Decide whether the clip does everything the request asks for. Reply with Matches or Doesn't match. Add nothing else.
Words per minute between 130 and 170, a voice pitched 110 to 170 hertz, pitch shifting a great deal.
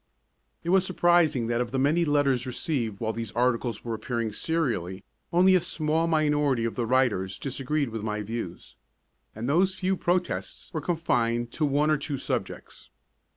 Matches